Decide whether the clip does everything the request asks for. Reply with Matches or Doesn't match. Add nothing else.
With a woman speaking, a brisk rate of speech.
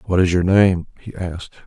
Doesn't match